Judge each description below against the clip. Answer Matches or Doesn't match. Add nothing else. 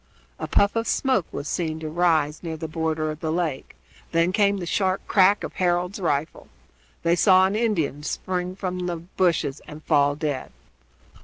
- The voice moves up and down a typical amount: Matches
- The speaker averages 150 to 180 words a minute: Matches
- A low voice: Doesn't match